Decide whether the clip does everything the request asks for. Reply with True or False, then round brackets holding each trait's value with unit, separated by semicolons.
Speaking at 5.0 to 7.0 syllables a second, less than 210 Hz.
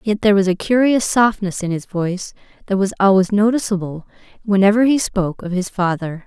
True (5.8 syllables/s; 200 Hz)